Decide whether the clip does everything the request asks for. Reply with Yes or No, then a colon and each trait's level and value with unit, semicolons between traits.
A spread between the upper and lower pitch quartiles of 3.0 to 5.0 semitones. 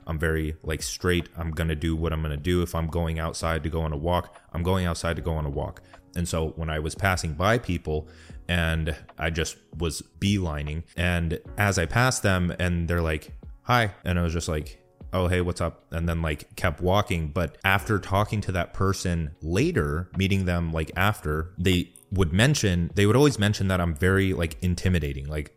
No: narrow, 2.6 semitones